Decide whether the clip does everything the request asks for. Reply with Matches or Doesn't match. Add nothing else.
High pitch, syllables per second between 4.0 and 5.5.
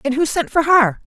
Matches